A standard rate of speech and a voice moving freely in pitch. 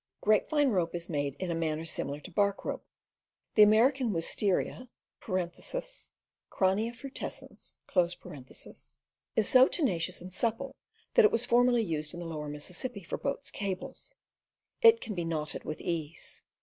Yes: average, 145 wpm; wide, 6.5 semitones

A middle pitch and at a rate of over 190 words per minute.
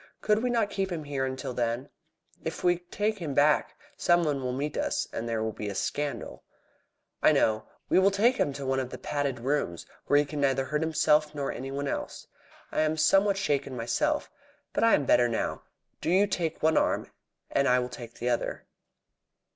Yes: medium, 145 Hz; average, 200 wpm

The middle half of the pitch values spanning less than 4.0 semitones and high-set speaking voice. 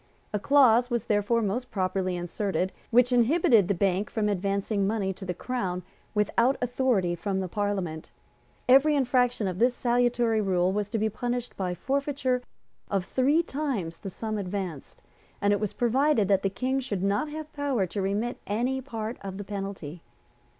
No: average, 4.4 semitones; high, 210 Hz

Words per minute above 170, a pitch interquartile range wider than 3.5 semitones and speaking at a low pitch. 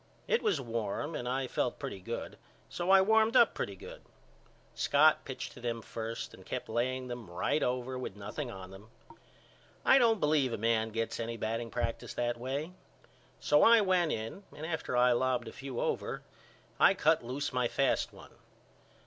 Yes: average, 180 wpm; average, 4.4 semitones; low, 125 Hz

